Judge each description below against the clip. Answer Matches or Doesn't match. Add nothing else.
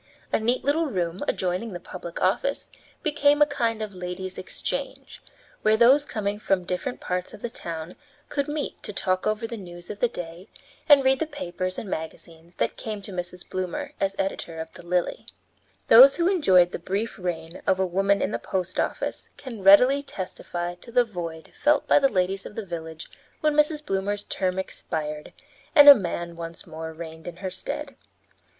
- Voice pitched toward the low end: Doesn't match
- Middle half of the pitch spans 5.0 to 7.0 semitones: Matches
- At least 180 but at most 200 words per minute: Matches